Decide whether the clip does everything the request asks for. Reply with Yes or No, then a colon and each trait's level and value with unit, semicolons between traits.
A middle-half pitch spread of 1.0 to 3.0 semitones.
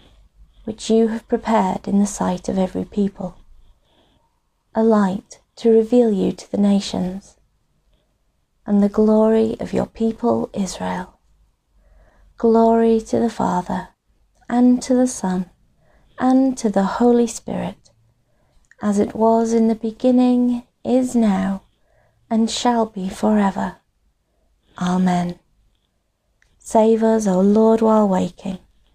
No: average, 3.4 semitones